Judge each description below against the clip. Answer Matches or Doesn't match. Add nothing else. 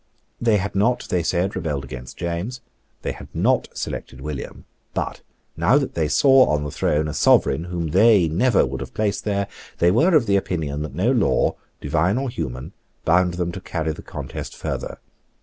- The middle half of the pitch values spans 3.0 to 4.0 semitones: Doesn't match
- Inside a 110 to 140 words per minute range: Doesn't match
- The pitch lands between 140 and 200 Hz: Doesn't match